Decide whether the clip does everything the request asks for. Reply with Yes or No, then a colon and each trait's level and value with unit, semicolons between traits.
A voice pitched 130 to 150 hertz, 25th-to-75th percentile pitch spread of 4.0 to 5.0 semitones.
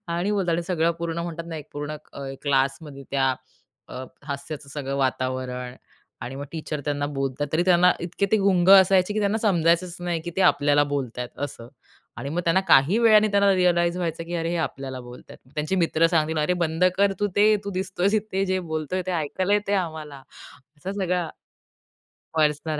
No: medium, 165 Hz; average, 4.4 semitones